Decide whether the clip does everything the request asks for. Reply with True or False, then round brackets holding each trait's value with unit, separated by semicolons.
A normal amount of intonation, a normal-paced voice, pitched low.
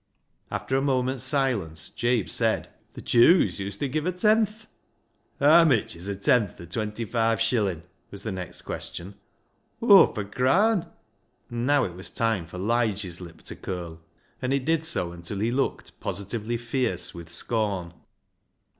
False (6.1 semitones; 170 wpm; 115 Hz)